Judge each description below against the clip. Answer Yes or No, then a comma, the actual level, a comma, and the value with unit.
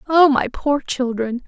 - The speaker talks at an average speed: Yes, average, 160 wpm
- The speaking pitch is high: Yes, very high, 265 Hz